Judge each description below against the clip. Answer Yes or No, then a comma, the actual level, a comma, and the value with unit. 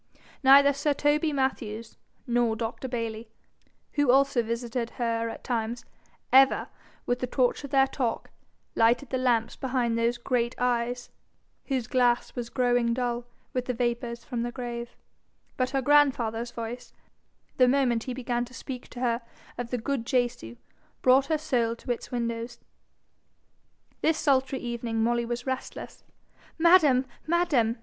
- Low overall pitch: No, high, 245 Hz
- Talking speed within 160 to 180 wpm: No, average, 145 wpm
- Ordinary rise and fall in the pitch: No, narrow, 2.0 semitones